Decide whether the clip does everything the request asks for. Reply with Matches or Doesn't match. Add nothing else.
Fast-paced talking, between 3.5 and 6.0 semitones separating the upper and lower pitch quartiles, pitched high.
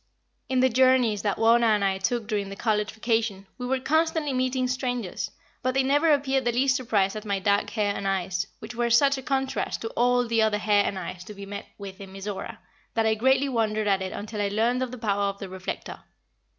Matches